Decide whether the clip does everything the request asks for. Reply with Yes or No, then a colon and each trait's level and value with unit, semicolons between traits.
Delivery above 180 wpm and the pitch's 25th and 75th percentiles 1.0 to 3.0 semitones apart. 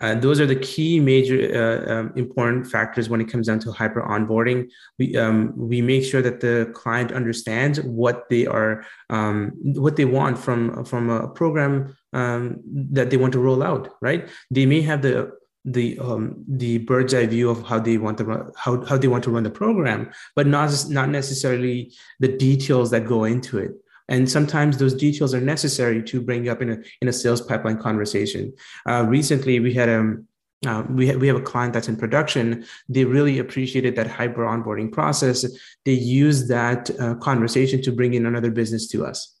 Yes: average, 200 wpm; narrow, 2.4 semitones